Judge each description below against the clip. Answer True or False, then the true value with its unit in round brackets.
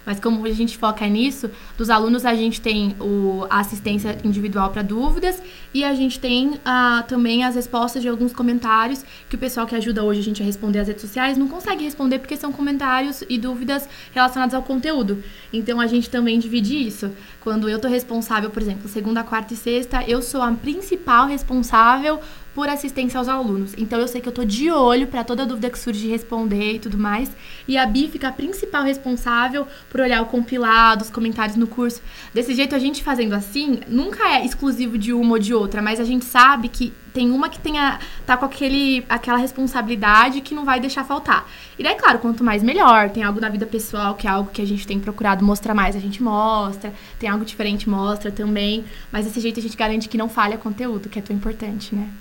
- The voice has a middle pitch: False (235 Hz)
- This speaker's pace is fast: True (215 wpm)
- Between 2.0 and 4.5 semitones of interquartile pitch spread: True (3.1 semitones)